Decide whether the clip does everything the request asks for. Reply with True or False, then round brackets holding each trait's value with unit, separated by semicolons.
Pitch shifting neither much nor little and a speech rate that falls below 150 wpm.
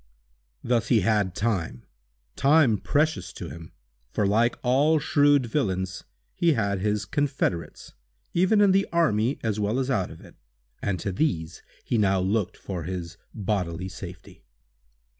False (6.6 semitones; 140 wpm)